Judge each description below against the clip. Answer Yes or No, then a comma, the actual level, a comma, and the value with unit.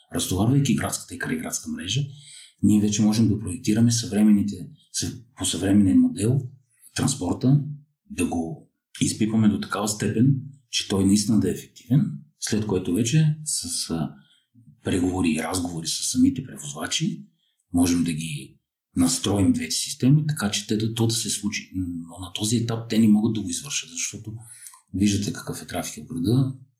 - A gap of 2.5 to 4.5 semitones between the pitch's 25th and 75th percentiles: No, average, 5.3 semitones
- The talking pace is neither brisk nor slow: Yes, average, 150 wpm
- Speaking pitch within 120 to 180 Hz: No, low, 110 Hz